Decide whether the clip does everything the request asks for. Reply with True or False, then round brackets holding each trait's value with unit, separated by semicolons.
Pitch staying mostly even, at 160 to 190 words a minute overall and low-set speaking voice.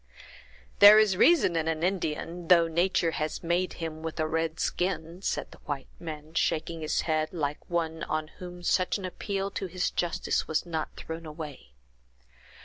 False (2.3 semitones; 170 wpm; 165 Hz)